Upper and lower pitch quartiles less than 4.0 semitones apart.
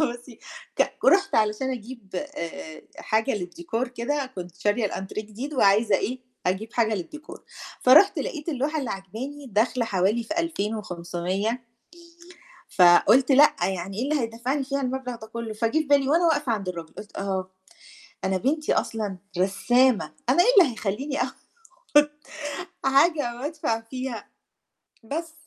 No: average, 5.3 semitones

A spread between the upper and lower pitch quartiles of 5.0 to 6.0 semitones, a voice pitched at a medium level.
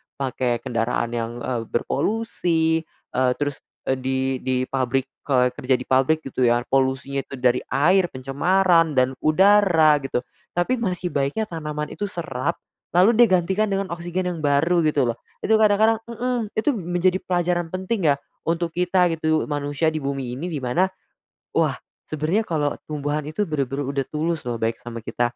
Yes: average, 5.3 semitones; medium, 155 Hz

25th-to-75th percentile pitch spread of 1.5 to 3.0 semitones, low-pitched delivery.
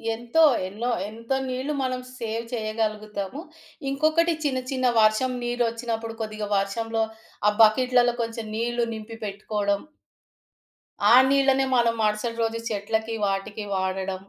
No: narrow, 2.6 semitones; high, 230 Hz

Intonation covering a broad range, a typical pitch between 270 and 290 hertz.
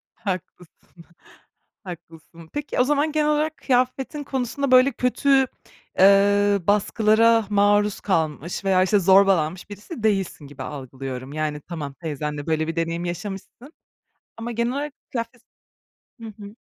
No: wide, 6.9 semitones; high, 200 Hz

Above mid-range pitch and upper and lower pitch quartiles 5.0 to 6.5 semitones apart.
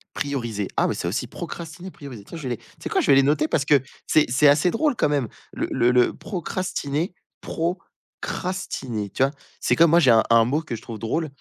No: medium, 140 Hz; wide, 5.6 semitones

